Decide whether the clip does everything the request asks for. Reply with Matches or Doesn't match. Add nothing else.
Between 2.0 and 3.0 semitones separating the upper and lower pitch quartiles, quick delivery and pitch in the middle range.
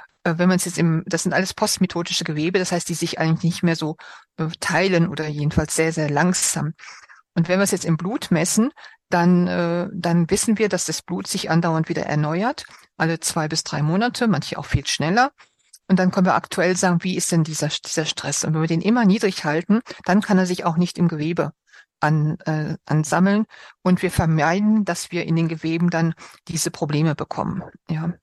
Matches